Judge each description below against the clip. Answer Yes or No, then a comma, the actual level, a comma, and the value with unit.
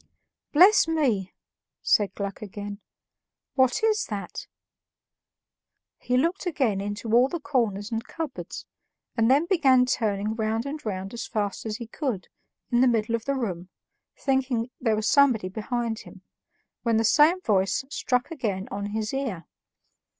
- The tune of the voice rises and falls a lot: No, average, 4.6 semitones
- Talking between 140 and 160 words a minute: Yes, average, 150 wpm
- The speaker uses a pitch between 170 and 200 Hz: No, high, 230 Hz